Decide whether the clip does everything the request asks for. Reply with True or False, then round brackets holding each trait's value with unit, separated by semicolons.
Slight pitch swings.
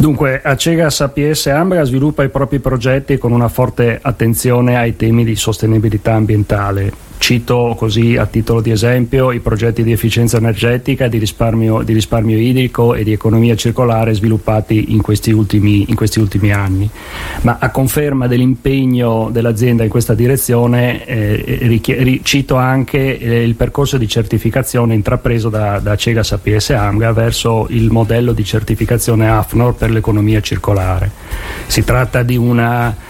True (2.3 semitones)